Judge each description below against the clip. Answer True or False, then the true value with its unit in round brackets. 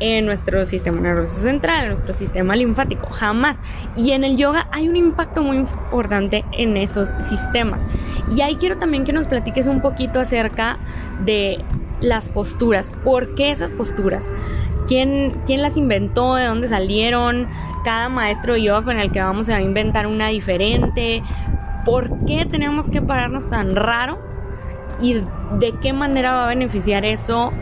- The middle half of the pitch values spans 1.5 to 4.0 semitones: False (4.8 semitones)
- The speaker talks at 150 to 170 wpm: True (165 wpm)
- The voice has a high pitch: True (235 Hz)